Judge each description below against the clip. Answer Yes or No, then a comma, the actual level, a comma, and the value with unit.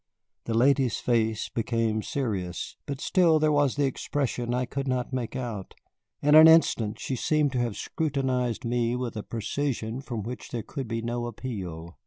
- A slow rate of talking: No, average, 175 wpm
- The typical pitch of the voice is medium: No, low, 125 Hz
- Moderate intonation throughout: Yes, average, 3.3 semitones